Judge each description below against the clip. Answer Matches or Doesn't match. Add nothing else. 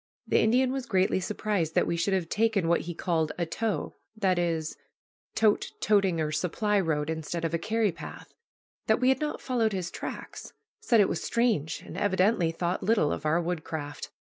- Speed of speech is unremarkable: Matches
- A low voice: Doesn't match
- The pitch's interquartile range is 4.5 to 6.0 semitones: Matches